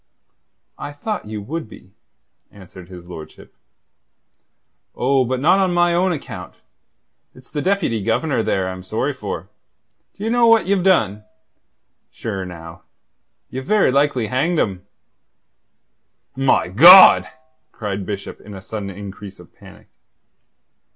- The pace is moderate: No, slow, 130 wpm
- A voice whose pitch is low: Yes, low, 115 Hz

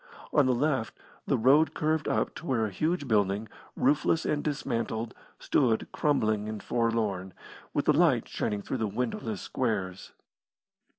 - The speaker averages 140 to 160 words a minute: Yes, average, 145 wpm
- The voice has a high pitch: No, low, 115 Hz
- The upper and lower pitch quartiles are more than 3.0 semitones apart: Yes, average, 5.2 semitones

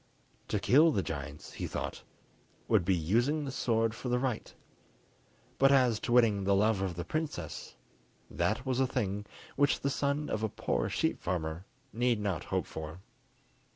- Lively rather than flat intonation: Yes, wide, 6.0 semitones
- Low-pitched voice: Yes, low, 110 Hz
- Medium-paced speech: Yes, average, 170 wpm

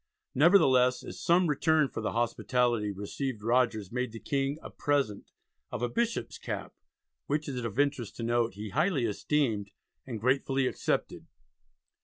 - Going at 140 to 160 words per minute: Yes, average, 155 wpm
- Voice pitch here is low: Yes, low, 125 Hz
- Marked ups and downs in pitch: No, average, 3.9 semitones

